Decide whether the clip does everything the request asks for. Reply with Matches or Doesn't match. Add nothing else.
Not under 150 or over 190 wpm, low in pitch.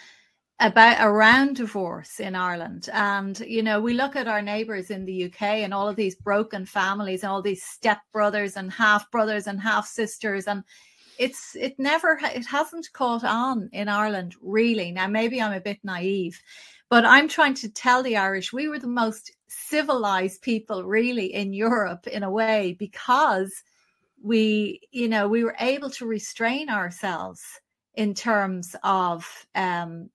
Doesn't match